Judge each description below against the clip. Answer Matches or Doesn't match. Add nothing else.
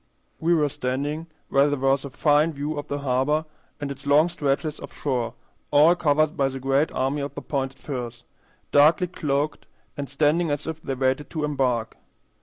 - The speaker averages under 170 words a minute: Doesn't match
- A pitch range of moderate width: Doesn't match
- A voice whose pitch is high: Doesn't match